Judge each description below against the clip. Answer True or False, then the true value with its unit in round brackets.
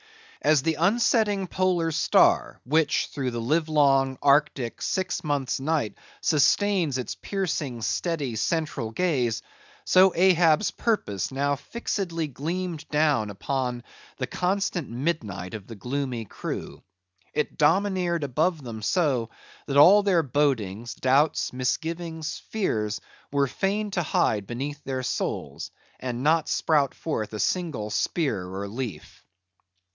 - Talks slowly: True (125 wpm)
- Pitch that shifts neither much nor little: False (5.7 semitones)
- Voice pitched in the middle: True (145 Hz)